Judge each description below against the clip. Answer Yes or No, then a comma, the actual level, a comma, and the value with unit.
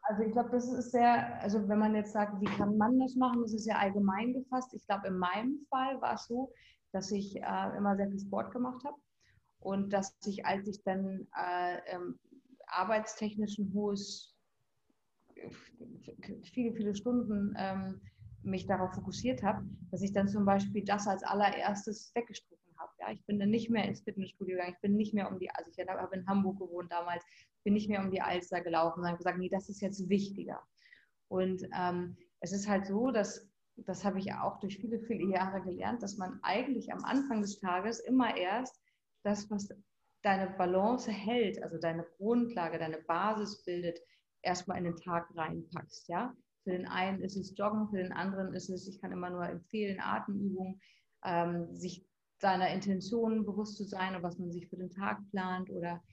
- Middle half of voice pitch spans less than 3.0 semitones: Yes, narrow, 2.6 semitones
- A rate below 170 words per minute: No, fast, 190 wpm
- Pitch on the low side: No, high, 200 Hz